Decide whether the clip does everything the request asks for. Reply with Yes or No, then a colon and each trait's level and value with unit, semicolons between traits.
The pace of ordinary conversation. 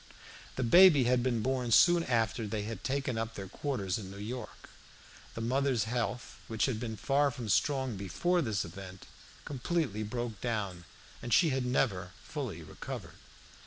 Yes: average, 165 wpm